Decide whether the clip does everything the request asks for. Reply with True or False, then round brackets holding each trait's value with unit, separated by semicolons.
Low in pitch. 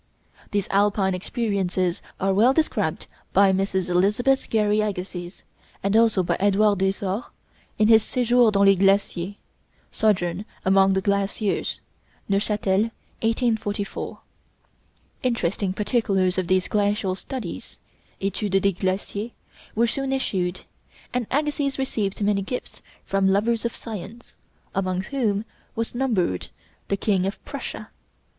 False (200 Hz)